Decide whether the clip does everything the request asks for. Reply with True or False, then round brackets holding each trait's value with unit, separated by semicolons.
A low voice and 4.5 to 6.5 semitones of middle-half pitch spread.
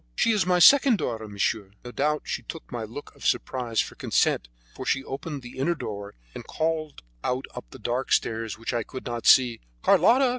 True (130 Hz; 5.5 semitones)